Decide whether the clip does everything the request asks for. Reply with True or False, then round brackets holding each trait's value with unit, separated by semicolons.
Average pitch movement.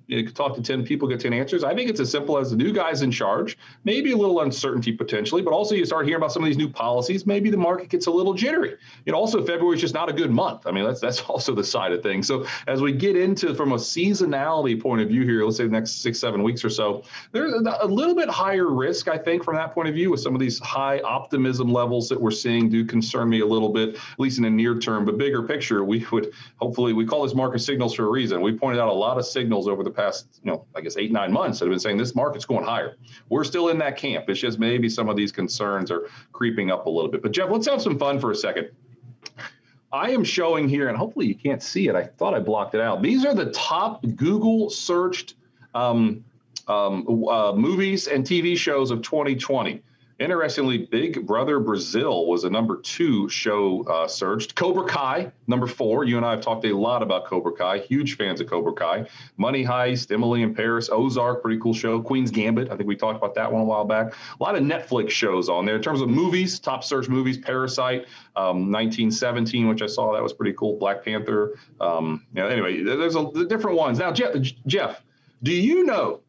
False (5.9 semitones)